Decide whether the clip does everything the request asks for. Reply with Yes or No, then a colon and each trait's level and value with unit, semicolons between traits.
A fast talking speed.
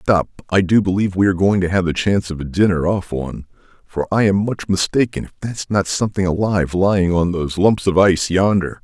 Yes: fast, 230 wpm